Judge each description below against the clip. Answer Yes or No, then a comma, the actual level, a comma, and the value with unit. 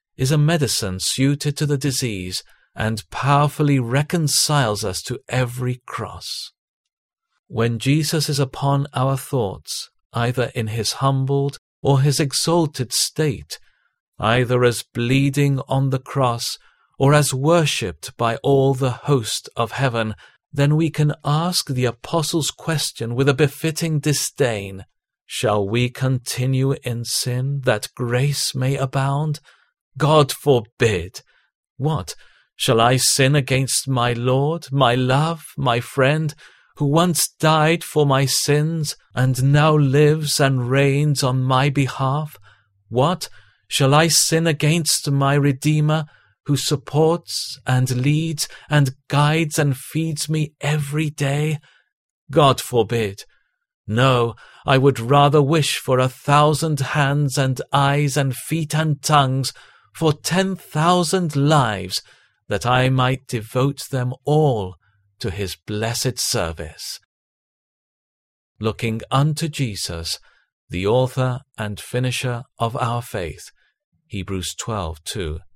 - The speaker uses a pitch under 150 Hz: Yes, low, 135 Hz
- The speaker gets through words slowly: Yes, slow, 120 wpm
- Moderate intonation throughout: Yes, average, 3.3 semitones